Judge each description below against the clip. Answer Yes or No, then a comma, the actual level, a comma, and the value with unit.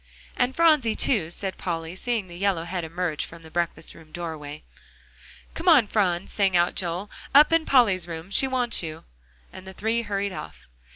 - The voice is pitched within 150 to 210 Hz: Yes, medium, 185 Hz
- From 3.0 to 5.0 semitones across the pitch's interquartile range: No, wide, 5.4 semitones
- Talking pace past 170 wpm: Yes, average, 180 wpm